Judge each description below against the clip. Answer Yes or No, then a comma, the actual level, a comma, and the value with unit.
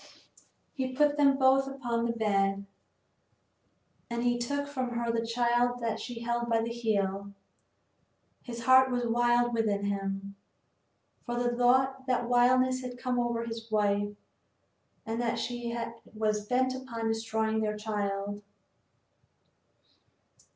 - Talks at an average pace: No, slow, 130 wpm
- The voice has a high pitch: Yes, high, 235 Hz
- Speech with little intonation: Yes, narrow, 2.2 semitones